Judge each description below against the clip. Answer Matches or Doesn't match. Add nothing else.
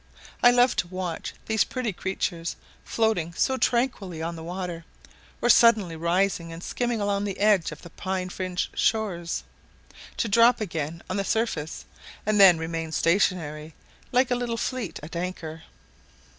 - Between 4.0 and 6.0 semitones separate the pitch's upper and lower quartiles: Matches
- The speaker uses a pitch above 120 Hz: Matches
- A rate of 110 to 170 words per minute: Matches